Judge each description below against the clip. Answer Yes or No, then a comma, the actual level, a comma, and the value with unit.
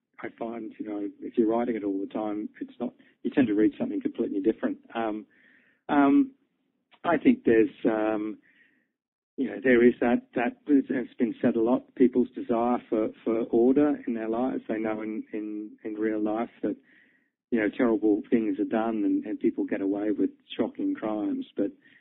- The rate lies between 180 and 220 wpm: Yes, average, 185 wpm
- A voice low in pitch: Yes, low, 120 Hz